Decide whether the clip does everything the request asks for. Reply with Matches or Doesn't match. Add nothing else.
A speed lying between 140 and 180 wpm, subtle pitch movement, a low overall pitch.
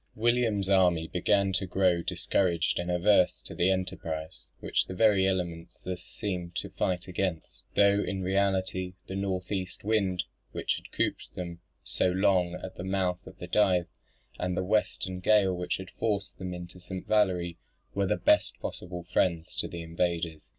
Matches